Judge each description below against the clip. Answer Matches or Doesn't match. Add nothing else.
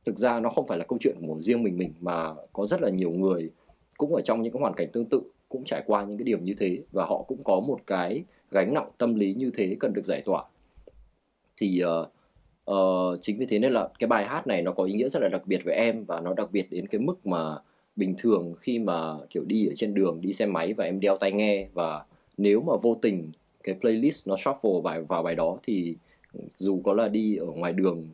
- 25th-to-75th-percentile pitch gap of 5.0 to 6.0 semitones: Doesn't match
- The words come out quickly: Matches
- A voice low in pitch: Matches